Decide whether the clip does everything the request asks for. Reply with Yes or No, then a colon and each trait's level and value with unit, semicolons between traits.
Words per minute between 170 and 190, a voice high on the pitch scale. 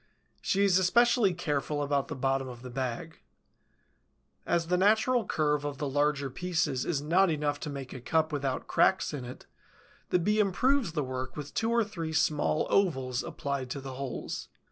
No: average, 180 wpm; medium, 150 Hz